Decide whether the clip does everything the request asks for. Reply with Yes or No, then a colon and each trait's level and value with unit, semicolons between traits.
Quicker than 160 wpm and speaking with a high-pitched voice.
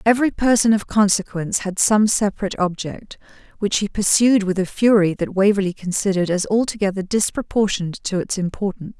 No: average, 155 wpm; high, 200 Hz